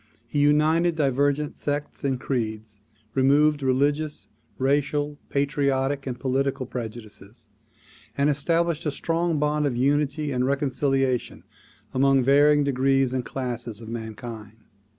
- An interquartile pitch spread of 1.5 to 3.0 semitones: Yes, narrow, 2.6 semitones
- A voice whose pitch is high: No, medium, 140 Hz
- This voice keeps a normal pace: No, slow, 115 wpm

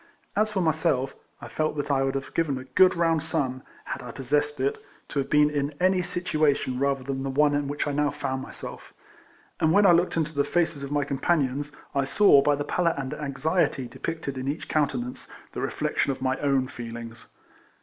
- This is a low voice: No, medium, 145 Hz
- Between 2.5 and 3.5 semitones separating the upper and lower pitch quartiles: Yes, average, 3.0 semitones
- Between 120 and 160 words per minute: No, fast, 205 wpm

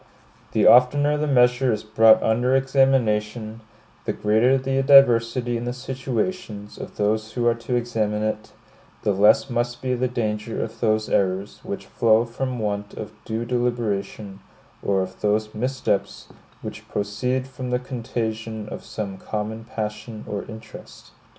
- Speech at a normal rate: Yes, average, 150 wpm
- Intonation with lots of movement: No, average, 2.9 semitones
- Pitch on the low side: Yes, low, 115 Hz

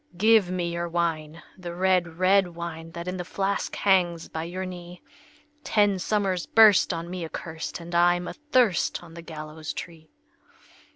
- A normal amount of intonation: No, narrow, 1.9 semitones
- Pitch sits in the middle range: Yes, medium, 175 Hz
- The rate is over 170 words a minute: No, average, 160 wpm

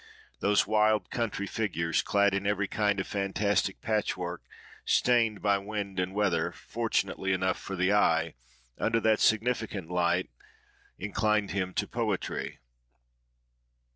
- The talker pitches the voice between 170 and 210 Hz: No, low, 100 Hz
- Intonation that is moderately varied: No, narrow, 2.3 semitones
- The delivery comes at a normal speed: No, slow, 125 wpm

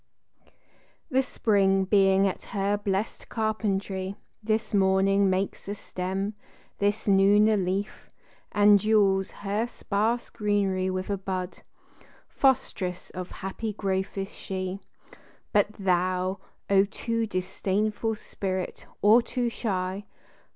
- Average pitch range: No, narrow, 1.8 semitones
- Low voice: No, high, 200 Hz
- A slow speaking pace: Yes, slow, 115 wpm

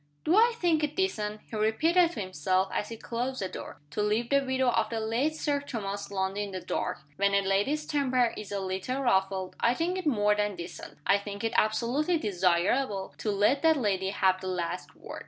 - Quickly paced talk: Yes, fast, 210 wpm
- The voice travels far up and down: Yes, wide, 5.9 semitones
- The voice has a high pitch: Yes, high, 215 Hz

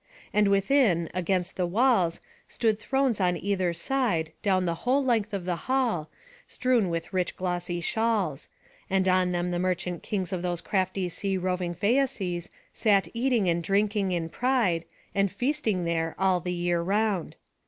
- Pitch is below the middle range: No, medium, 185 Hz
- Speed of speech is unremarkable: Yes, average, 160 wpm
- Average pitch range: Yes, average, 3.8 semitones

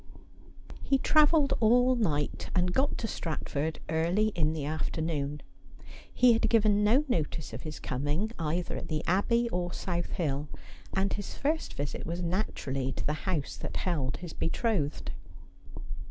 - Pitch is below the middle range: No, medium, 175 Hz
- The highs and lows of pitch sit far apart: Yes, wide, 6.2 semitones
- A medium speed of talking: Yes, average, 150 wpm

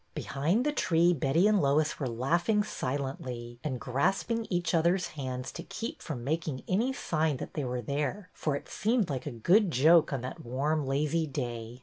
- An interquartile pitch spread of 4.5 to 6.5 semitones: Yes, average, 5.2 semitones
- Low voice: No, medium, 150 Hz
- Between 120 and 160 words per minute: No, average, 180 wpm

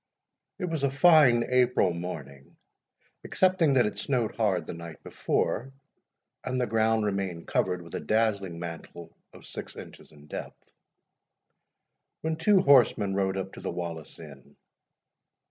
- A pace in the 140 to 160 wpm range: Yes, average, 145 wpm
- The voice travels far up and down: Yes, wide, 7.0 semitones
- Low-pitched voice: Yes, low, 105 Hz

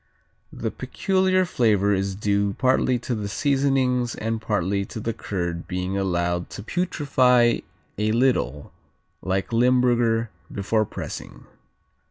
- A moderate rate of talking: No, slow, 120 wpm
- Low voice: Yes, low, 110 Hz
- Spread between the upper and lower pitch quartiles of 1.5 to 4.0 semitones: No, average, 4.4 semitones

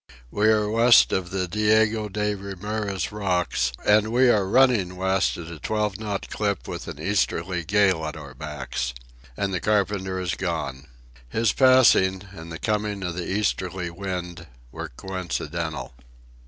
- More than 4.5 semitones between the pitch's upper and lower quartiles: No, average, 3.2 semitones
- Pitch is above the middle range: No, very low, 95 Hz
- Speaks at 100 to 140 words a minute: No, average, 155 wpm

